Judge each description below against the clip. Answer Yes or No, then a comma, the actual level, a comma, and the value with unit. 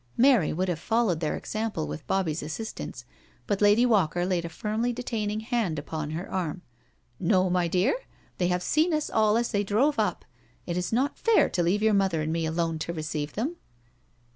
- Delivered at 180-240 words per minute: Yes, average, 195 wpm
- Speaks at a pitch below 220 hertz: Yes, high, 190 Hz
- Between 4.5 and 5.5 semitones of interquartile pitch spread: Yes, average, 4.9 semitones